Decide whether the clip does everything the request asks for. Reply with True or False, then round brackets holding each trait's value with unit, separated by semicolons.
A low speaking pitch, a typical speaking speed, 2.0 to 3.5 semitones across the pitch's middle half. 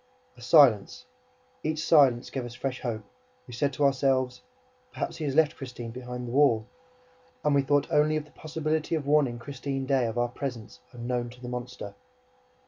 True (130 Hz; 180 wpm; 3.0 semitones)